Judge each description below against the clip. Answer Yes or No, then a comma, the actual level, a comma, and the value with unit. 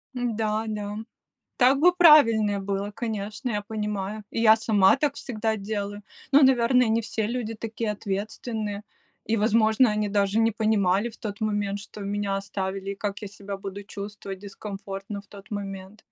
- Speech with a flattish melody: Yes, narrow, 1.8 semitones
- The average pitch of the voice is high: Yes, high, 210 Hz